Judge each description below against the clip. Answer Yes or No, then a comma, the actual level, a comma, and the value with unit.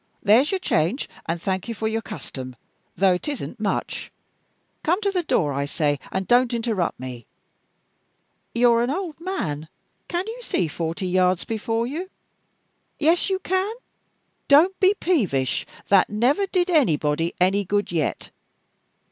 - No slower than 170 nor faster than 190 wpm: No, average, 145 wpm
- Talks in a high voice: Yes, high, 225 Hz